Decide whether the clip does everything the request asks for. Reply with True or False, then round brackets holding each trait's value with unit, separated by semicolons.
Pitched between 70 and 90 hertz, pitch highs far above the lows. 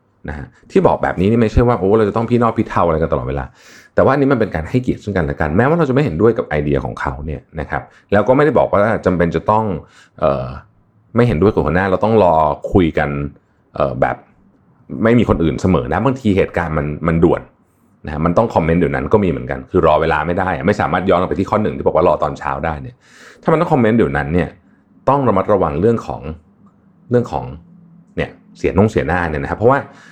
True (85 Hz; 6.9 semitones)